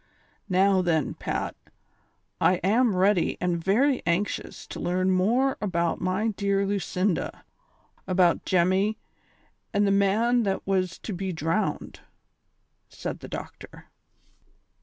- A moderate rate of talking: No, slow, 120 wpm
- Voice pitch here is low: No, high, 190 Hz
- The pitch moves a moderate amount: No, narrow, 2.2 semitones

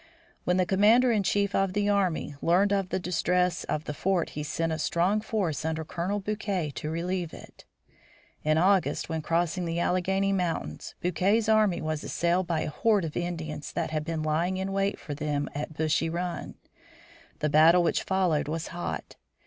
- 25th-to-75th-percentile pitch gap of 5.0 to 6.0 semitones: No, average, 3.4 semitones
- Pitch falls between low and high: Yes, medium, 175 Hz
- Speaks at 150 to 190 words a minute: Yes, average, 180 wpm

